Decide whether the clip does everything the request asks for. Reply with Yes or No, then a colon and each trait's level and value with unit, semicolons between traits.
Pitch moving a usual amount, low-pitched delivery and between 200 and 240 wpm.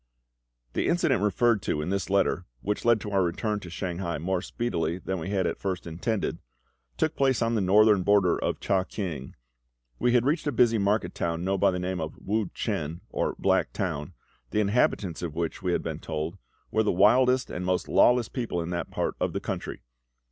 Yes: average, 4.0 semitones; very low, 95 Hz; fast, 205 wpm